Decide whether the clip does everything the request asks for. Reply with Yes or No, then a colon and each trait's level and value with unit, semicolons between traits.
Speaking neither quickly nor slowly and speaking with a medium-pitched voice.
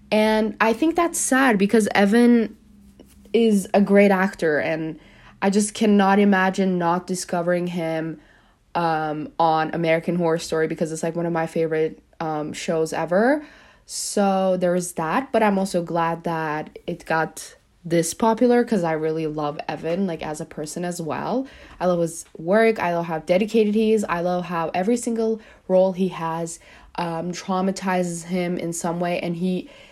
Yes: average, 165 wpm; medium, 175 Hz